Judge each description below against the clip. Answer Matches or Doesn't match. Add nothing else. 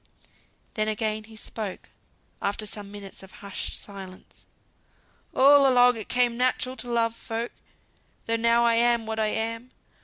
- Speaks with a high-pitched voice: Matches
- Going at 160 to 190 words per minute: Doesn't match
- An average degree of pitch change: Doesn't match